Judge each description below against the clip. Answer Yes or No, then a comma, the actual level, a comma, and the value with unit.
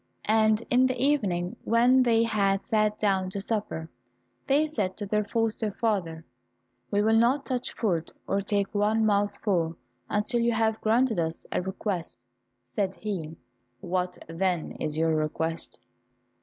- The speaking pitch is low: No, high, 205 Hz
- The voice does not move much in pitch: No, average, 3.8 semitones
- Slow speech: No, average, 145 wpm